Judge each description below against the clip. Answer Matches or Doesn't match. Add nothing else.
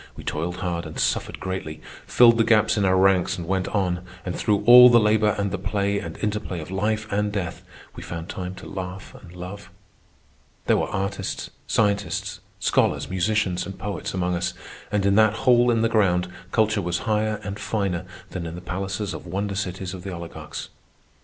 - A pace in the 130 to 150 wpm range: Doesn't match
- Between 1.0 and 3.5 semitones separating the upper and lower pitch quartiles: Matches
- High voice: Doesn't match